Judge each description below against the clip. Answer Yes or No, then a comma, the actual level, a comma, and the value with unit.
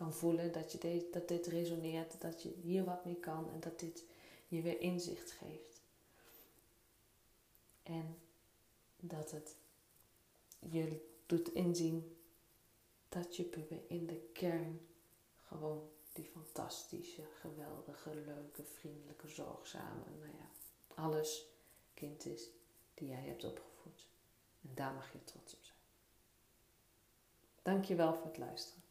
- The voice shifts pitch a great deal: Yes, wide, 6.0 semitones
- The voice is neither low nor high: Yes, medium, 160 Hz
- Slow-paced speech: Yes, slow, 125 wpm